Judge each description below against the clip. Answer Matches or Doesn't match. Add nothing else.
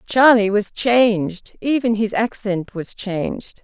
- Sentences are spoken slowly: Matches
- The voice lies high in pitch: Matches